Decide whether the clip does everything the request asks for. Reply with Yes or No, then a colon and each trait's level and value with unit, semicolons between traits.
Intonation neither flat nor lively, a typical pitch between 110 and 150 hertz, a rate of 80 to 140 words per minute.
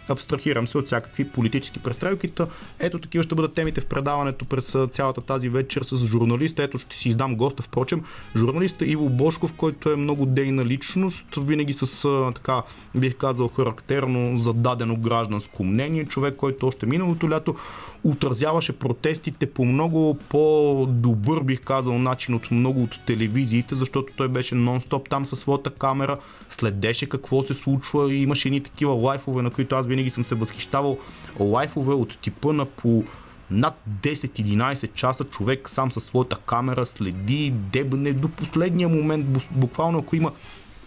No: average, 3.1 semitones; low, 135 Hz; average, 155 wpm